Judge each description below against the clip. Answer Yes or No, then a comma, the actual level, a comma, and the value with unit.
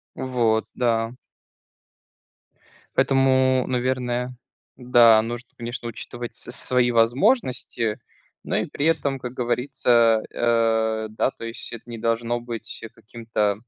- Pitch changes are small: Yes, narrow, 1.8 semitones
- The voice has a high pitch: No, low, 120 Hz